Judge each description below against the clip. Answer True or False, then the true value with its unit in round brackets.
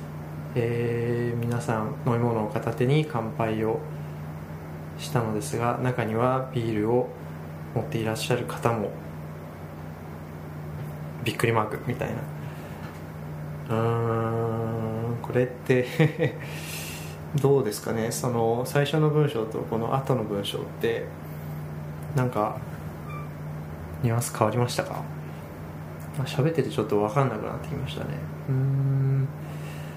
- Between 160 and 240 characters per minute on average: True (235 characters per minute)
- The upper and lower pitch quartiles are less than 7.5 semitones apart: False (8.0 semitones)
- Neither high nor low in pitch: False (110 Hz)